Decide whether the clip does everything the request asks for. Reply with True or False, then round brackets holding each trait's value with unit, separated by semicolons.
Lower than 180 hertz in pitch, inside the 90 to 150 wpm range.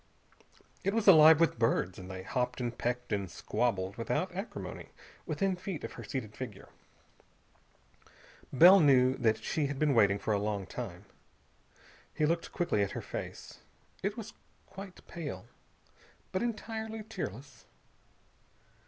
True (135 Hz; 140 wpm)